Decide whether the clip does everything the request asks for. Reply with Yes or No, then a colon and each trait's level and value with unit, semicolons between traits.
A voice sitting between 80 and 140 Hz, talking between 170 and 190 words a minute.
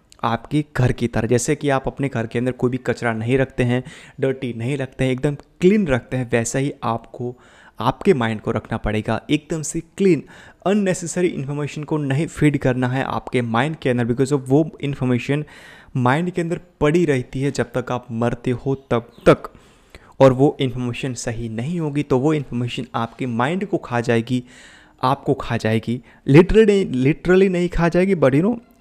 Yes: low, 135 Hz; average, 185 wpm